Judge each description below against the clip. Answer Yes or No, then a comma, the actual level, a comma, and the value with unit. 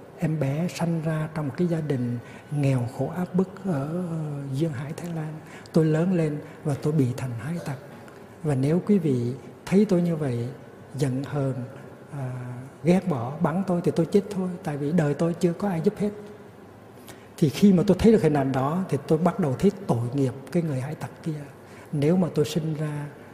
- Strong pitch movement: No, average, 4.3 semitones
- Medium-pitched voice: Yes, medium, 155 Hz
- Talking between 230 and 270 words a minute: No, average, 210 wpm